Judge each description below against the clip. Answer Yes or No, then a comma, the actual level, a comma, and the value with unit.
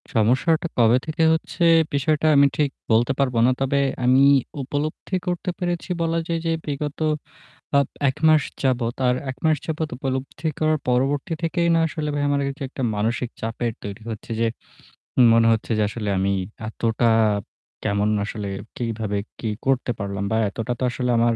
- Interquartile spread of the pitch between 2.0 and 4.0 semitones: No, average, 4.9 semitones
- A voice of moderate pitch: No, low, 130 Hz